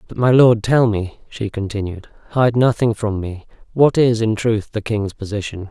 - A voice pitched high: No, low, 110 Hz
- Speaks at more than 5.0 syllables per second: No, 4.7 syllables/s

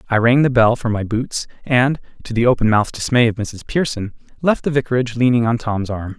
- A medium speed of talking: No, fast, 225 wpm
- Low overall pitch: Yes, low, 120 Hz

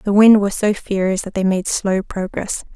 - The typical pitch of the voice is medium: No, high, 200 Hz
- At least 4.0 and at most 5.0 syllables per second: Yes, 4.6 syllables/s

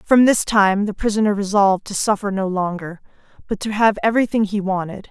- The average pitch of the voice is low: No, high, 200 Hz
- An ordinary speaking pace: Yes, average, 190 wpm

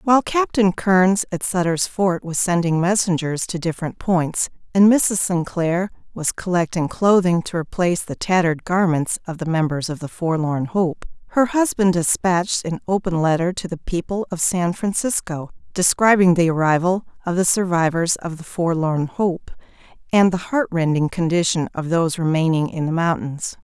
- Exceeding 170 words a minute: No, average, 160 wpm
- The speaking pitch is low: No, medium, 175 Hz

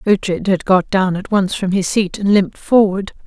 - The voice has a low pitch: No, high, 190 Hz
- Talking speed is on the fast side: Yes, fast, 220 wpm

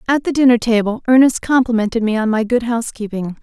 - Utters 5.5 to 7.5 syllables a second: Yes, 6.2 syllables/s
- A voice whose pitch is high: Yes, high, 235 Hz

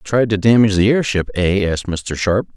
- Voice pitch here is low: Yes, low, 100 Hz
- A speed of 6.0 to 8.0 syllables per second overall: No, 5.4 syllables/s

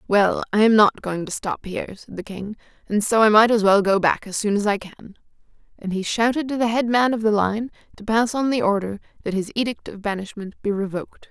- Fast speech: Yes, fast, 245 wpm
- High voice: Yes, high, 210 Hz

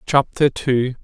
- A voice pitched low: Yes, low, 130 Hz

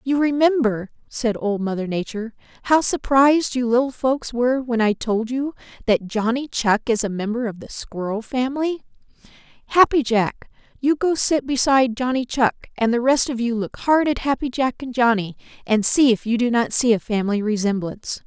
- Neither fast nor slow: Yes, average, 185 wpm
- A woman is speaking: Yes, female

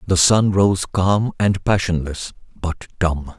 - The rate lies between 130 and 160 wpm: Yes, average, 140 wpm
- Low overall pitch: Yes, very low, 90 Hz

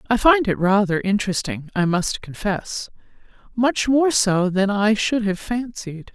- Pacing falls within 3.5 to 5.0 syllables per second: Yes, 4.1 syllables/s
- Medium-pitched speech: No, high, 210 Hz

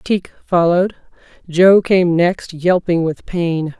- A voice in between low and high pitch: Yes, medium, 175 Hz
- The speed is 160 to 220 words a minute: No, slow, 125 wpm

